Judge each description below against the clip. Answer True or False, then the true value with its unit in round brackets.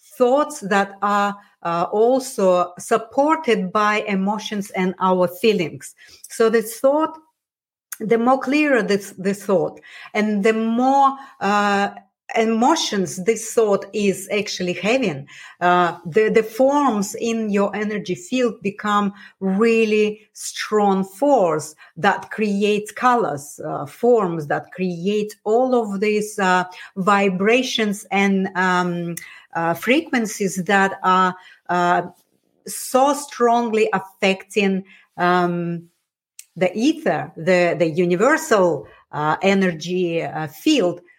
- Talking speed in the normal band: False (110 wpm)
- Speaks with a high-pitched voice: True (205 Hz)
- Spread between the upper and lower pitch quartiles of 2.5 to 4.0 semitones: True (3.7 semitones)